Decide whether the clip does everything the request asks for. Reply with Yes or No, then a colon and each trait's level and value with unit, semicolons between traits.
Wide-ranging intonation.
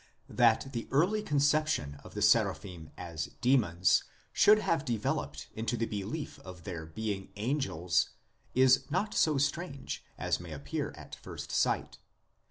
Yes: wide, 8.5 semitones